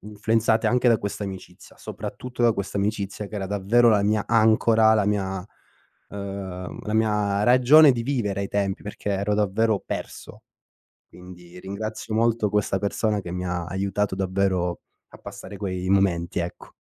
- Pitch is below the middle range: Yes, low, 100 Hz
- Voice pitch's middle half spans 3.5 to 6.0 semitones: No, narrow, 2.4 semitones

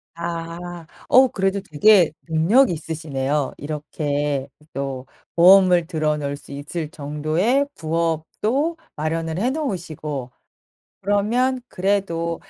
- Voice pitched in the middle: Yes, medium, 165 Hz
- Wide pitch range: No, average, 4.5 semitones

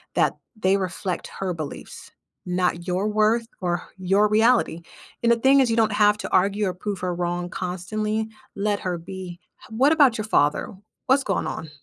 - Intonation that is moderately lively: Yes, average, 3.5 semitones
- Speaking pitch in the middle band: No, high, 195 Hz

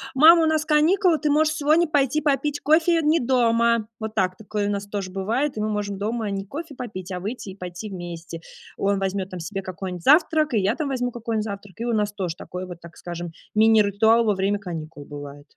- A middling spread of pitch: No, wide, 6.7 semitones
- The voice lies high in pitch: Yes, high, 215 Hz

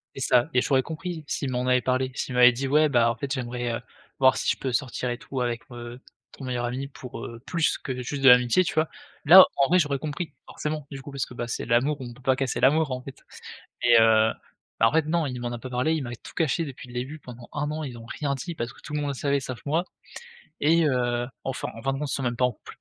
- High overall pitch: No, low, 130 Hz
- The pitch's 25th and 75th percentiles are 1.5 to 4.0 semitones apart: Yes, average, 3.1 semitones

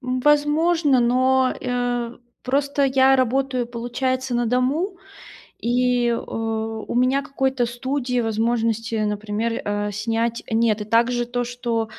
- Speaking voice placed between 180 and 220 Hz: No, high, 245 Hz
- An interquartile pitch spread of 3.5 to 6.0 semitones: No, narrow, 2.4 semitones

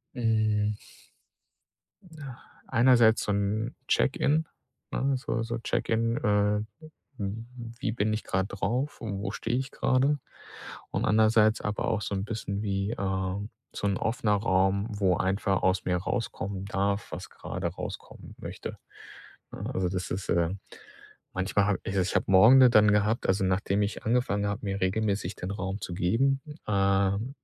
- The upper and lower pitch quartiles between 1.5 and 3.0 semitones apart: Yes, average, 2.7 semitones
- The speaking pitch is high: No, low, 105 Hz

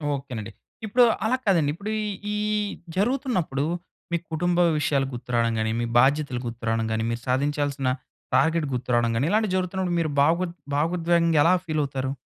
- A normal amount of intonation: No, wide, 5.7 semitones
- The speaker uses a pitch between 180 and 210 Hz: No, medium, 150 Hz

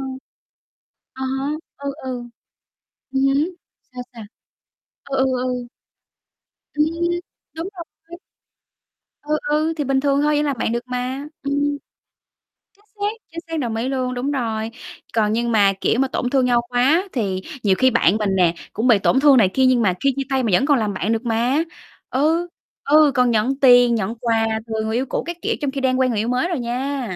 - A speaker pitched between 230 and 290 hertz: Yes, very high, 255 Hz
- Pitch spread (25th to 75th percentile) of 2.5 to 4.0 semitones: Yes, average, 3.4 semitones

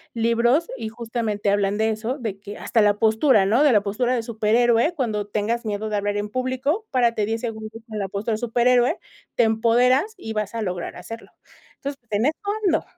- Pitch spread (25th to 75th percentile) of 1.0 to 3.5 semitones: Yes, average, 2.7 semitones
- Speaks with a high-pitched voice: Yes, high, 225 Hz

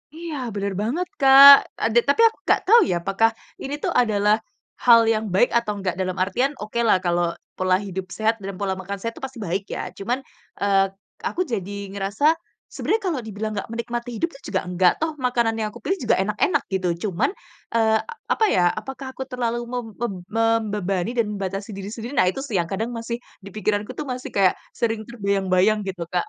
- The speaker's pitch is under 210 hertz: No, high, 215 Hz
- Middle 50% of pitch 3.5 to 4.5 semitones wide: Yes, average, 3.8 semitones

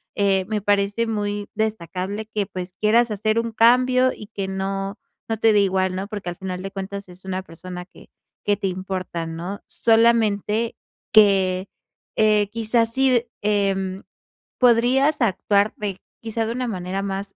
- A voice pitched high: Yes, high, 205 Hz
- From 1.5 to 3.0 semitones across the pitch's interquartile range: Yes, average, 2.7 semitones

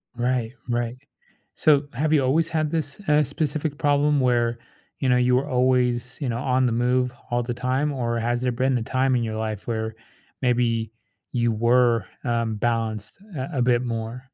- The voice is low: Yes, low, 125 Hz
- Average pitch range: No, narrow, 2.3 semitones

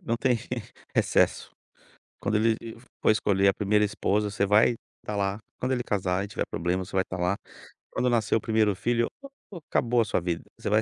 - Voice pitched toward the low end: Yes, low, 105 Hz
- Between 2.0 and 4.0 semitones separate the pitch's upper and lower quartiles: Yes, average, 2.9 semitones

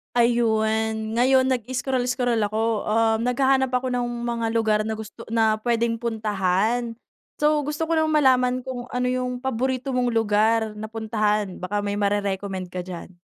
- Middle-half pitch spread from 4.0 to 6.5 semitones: No, average, 2.7 semitones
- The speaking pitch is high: Yes, high, 230 Hz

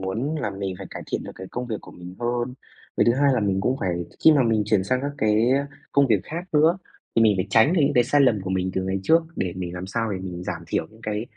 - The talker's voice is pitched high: No, low, 110 Hz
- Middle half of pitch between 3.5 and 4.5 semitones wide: No, average, 5.2 semitones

